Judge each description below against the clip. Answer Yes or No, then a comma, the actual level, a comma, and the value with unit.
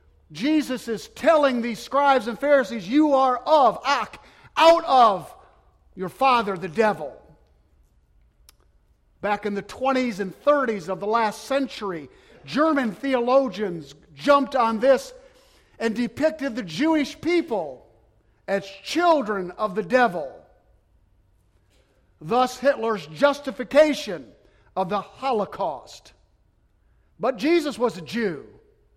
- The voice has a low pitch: No, high, 230 Hz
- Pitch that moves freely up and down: Yes, wide, 7.5 semitones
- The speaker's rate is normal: No, slow, 110 wpm